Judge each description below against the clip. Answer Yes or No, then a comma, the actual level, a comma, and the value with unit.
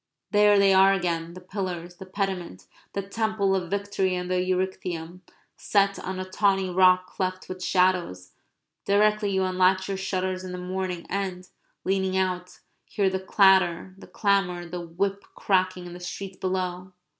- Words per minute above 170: No, average, 160 wpm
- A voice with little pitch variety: Yes, narrow, 1.3 semitones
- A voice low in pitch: No, medium, 185 Hz